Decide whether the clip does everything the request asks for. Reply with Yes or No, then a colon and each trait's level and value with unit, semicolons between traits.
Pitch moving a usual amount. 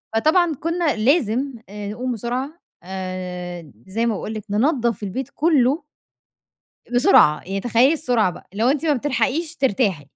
No: wide, 5.8 semitones